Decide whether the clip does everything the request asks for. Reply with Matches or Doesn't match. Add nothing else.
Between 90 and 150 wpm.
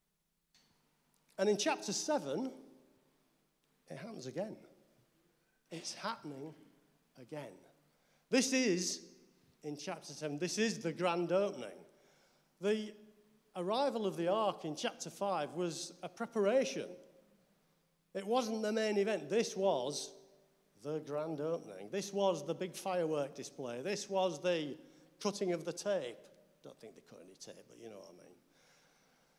Matches